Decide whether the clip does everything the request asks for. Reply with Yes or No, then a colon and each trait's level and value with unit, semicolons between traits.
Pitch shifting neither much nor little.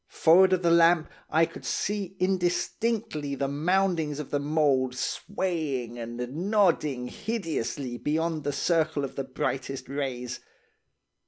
Yes: average, 4.7 semitones